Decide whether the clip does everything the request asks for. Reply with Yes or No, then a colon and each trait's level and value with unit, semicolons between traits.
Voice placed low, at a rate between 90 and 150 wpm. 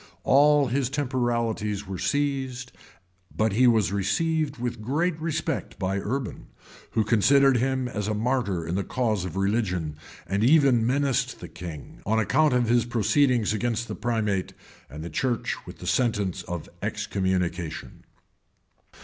Yes: low, 115 Hz; average, 145 wpm